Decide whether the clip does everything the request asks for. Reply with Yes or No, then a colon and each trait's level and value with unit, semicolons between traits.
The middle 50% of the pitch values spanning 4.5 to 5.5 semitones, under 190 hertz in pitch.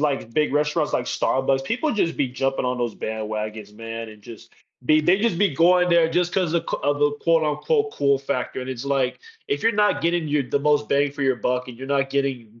Yes: average, 4.8 semitones; medium, 140 Hz